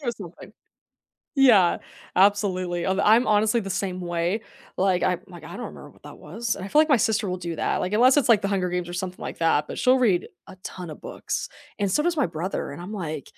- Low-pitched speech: No, high, 190 Hz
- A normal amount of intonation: Yes, average, 3.9 semitones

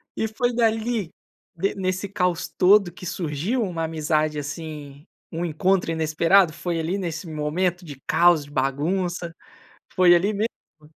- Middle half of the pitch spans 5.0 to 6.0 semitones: No, average, 3.5 semitones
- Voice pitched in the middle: Yes, medium, 170 Hz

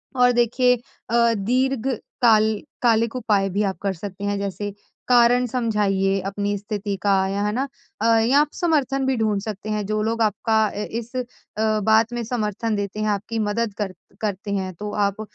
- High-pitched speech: Yes, high, 215 Hz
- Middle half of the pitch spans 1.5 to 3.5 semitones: Yes, narrow, 2.6 semitones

